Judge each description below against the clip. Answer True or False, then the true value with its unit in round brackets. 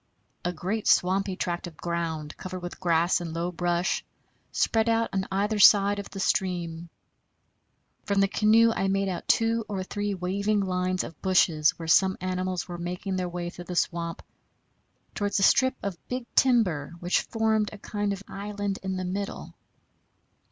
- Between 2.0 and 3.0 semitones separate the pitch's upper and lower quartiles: True (2.6 semitones)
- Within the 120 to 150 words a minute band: False (165 wpm)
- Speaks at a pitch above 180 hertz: True (190 Hz)